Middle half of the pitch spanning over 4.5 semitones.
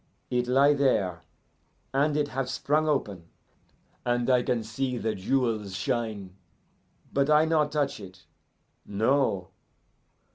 Yes: average, 5.1 semitones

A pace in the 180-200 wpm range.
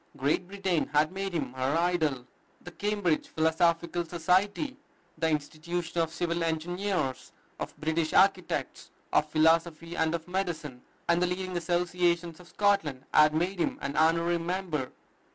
No: average, 140 wpm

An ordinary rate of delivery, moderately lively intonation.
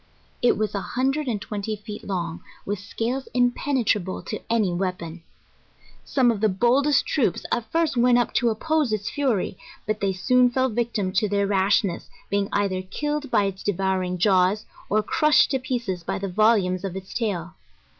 Yes: average, 175 wpm; average, 4.4 semitones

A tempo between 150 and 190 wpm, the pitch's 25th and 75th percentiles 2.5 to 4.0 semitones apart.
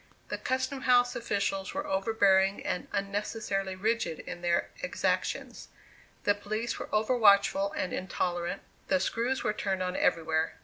No: average, 140 wpm; average, 3.4 semitones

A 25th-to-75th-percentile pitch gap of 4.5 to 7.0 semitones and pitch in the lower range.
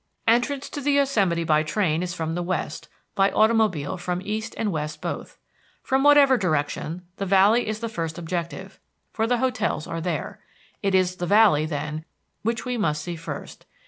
No: wide, 5.4 semitones; medium, 185 Hz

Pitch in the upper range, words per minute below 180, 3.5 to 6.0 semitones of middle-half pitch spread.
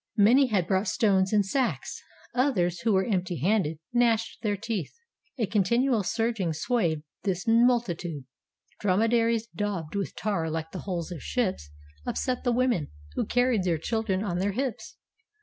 Yes: high, 205 Hz; average, 155 wpm; average, 4.6 semitones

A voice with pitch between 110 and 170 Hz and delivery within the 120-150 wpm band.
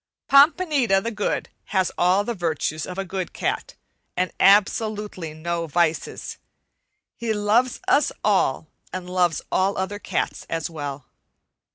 No: high, 190 Hz; slow, 135 wpm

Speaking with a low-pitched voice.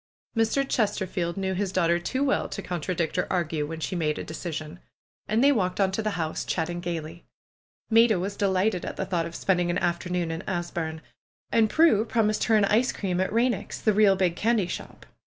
No: medium, 185 Hz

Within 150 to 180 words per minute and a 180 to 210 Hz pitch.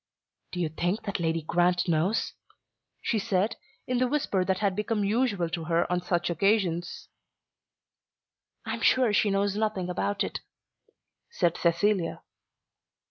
No: average, 140 wpm; high, 190 Hz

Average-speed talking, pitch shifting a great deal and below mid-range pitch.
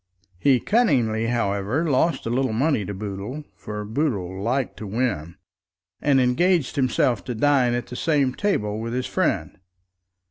No: average, 150 wpm; average, 4.7 semitones; low, 125 Hz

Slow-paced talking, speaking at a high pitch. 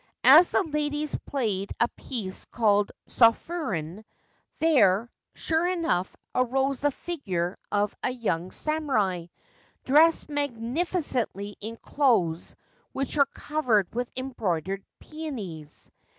Yes: slow, 110 wpm; high, 245 Hz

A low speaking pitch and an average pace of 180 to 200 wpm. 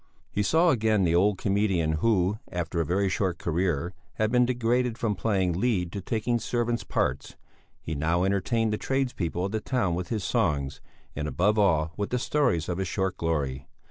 Yes: very low, 95 Hz; average, 185 wpm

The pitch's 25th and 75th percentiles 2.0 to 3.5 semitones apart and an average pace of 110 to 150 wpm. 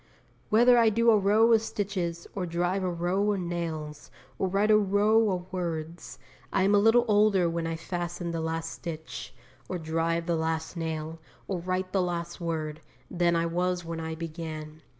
No: average, 3.1 semitones; average, 185 wpm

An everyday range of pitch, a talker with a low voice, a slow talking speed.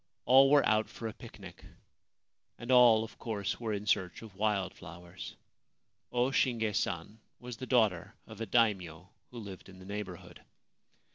No: average, 3.8 semitones; low, 110 Hz; average, 160 wpm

